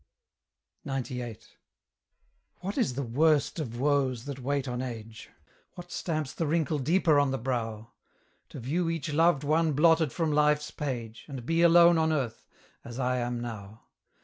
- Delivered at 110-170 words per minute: Yes, average, 155 wpm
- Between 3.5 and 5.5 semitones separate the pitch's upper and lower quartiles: Yes, average, 4.6 semitones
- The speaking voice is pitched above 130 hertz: Yes, medium, 140 Hz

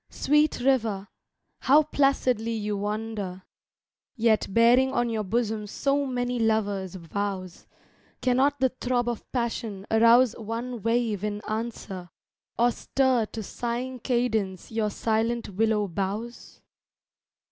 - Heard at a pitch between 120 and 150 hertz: No, high, 225 Hz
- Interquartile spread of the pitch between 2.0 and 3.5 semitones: Yes, average, 2.9 semitones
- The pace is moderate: No, slow, 115 wpm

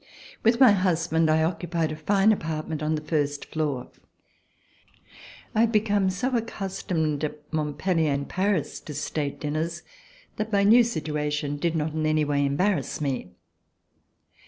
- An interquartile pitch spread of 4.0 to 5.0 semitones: Yes, average, 4.5 semitones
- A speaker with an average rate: Yes, average, 145 wpm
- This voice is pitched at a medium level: Yes, medium, 160 Hz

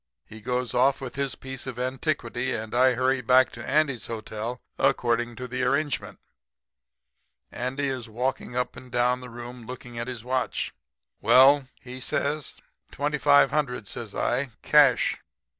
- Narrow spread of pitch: Yes, narrow, 1.7 semitones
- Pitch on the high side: No, low, 125 Hz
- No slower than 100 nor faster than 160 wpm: Yes, average, 150 wpm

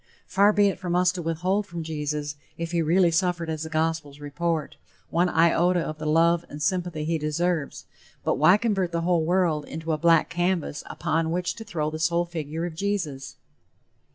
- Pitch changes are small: Yes, narrow, 2.3 semitones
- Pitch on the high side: No, medium, 165 Hz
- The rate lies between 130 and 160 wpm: No, average, 190 wpm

